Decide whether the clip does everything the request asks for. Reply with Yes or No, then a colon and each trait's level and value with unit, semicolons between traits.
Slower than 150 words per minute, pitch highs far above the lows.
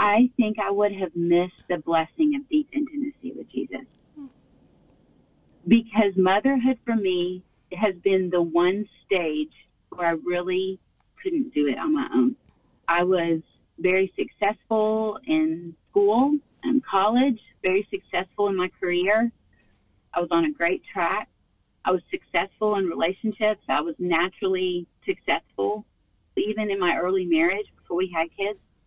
No: average, 140 wpm; average, 5.0 semitones